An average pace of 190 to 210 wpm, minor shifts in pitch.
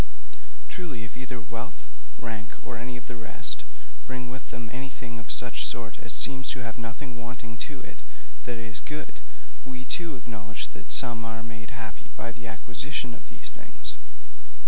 No: average, 170 wpm; narrow, 1.8 semitones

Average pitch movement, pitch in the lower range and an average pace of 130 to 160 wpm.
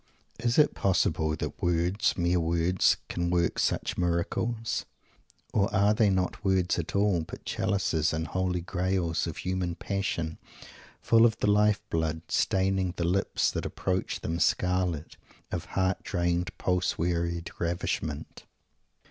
No: narrow, 2.3 semitones; very low, 90 Hz; average, 140 wpm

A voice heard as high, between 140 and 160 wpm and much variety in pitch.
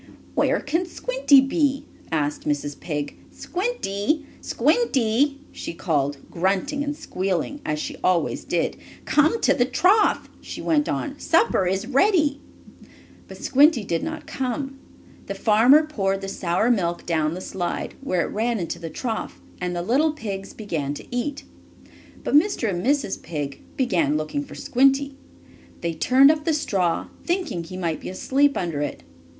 Yes: high, 240 Hz; average, 155 wpm; wide, 8.8 semitones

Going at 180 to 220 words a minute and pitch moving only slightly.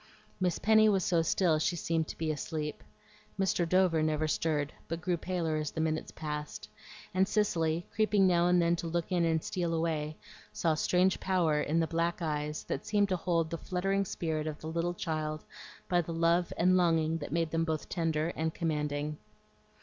Yes: average, 190 wpm; narrow, 2.2 semitones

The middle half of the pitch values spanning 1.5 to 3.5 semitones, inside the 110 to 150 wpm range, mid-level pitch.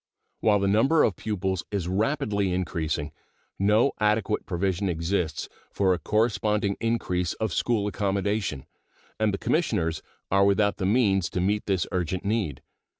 No: average, 2.8 semitones; average, 145 wpm; low, 100 Hz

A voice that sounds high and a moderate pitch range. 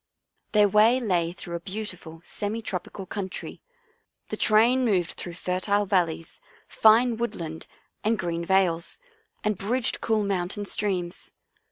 Yes: high, 195 Hz; average, 3.6 semitones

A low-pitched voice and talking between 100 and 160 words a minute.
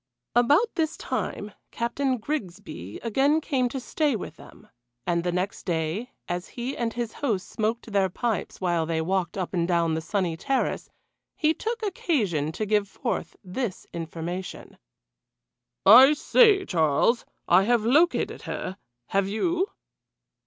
No: high, 210 Hz; average, 145 wpm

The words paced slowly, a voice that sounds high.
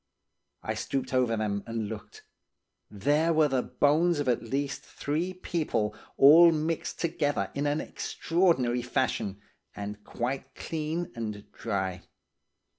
No: slow, 125 wpm; low, 135 Hz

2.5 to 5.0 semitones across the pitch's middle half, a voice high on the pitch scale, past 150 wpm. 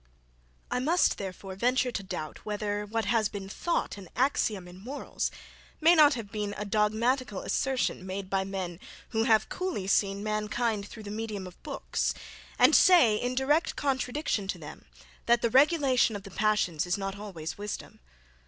Yes: average, 4.2 semitones; high, 210 Hz; average, 170 wpm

